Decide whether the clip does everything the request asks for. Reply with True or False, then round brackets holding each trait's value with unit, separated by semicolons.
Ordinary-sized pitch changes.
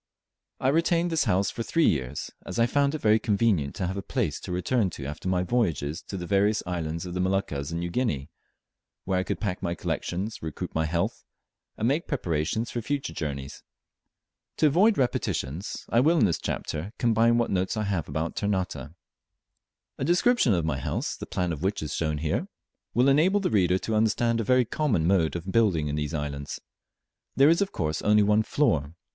False (6.7 semitones)